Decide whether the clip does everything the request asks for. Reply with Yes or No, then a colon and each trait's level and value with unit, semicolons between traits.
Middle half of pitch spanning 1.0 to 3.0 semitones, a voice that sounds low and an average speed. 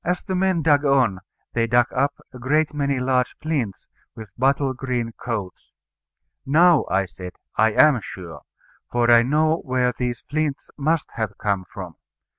No: average, 4.7 semitones; low, 130 Hz; average, 160 wpm